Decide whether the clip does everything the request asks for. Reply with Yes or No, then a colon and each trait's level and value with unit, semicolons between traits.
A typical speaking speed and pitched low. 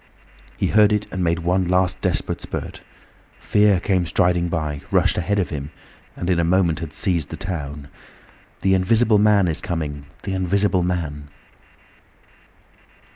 Yes: average, 150 wpm; very low, 90 Hz